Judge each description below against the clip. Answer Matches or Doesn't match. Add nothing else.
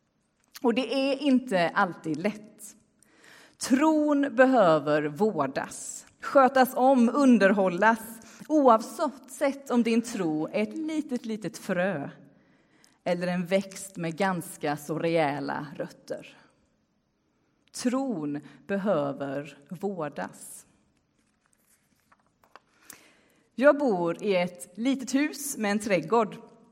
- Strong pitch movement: Matches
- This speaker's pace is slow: Matches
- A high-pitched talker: Matches